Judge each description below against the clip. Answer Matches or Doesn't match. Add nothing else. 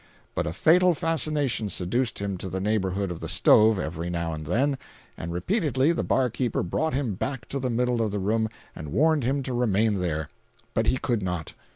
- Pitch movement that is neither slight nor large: Doesn't match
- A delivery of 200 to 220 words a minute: Matches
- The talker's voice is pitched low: Matches